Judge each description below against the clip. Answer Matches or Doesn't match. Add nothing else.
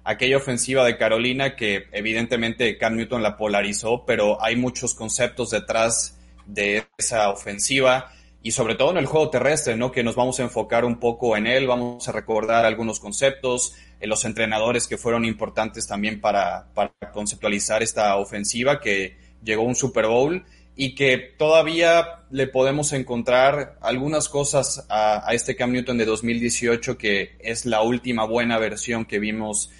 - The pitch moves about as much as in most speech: Matches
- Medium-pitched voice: Doesn't match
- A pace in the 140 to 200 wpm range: Matches